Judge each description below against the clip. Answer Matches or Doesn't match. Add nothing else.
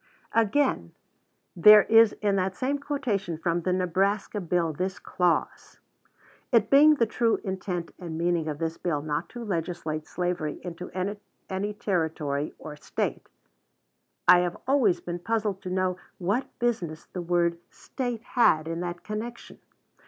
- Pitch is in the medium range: Matches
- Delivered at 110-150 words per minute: Matches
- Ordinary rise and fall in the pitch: Matches